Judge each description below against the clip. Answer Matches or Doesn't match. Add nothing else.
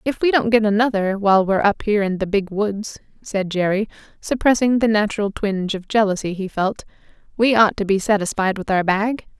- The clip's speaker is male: Doesn't match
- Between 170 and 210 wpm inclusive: Matches